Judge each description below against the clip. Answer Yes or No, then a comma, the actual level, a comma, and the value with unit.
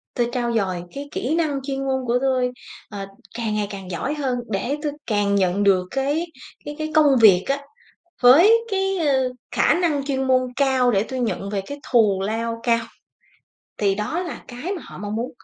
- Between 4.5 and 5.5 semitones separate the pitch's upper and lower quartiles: Yes, average, 5.2 semitones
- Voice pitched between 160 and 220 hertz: No, very high, 250 Hz